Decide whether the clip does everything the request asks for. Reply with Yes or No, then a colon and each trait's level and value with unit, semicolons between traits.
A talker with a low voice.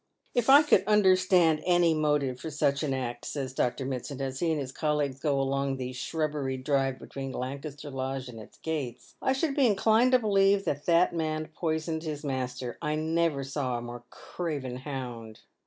No: medium, 145 Hz